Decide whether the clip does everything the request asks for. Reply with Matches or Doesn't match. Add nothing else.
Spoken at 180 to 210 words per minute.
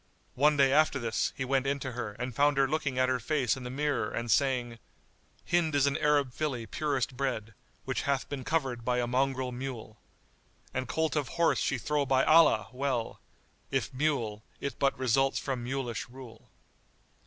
Matches